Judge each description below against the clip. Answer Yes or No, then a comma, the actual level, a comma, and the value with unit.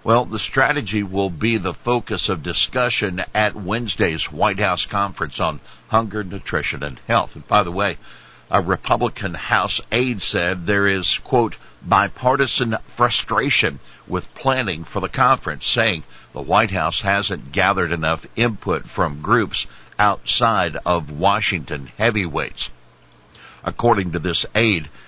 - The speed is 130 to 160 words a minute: Yes, slow, 135 wpm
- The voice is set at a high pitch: No, low, 100 Hz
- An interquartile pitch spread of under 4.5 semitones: No, average, 4.8 semitones